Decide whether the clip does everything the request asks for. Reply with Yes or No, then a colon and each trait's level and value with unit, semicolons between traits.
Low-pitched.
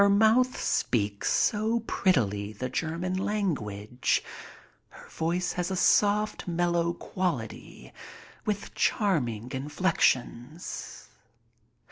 No: medium, 170 Hz